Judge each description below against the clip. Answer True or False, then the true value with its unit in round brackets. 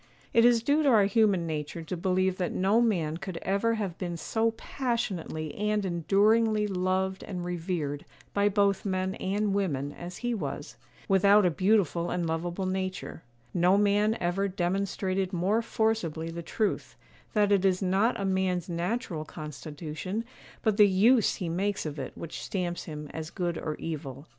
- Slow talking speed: False (165 wpm)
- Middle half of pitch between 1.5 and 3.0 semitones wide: False (3.4 semitones)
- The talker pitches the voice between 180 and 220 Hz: True (190 Hz)